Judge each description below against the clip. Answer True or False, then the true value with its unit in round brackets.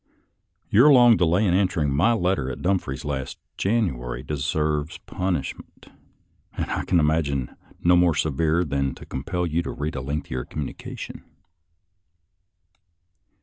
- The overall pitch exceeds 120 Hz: False (80 Hz)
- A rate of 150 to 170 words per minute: False (140 wpm)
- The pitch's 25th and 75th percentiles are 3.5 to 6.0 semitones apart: True (4.4 semitones)